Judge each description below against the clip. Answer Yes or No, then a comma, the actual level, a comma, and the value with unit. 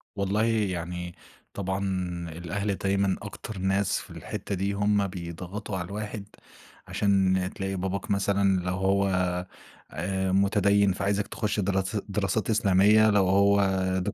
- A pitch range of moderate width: No, narrow, 1.4 semitones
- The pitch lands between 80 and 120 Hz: Yes, low, 100 Hz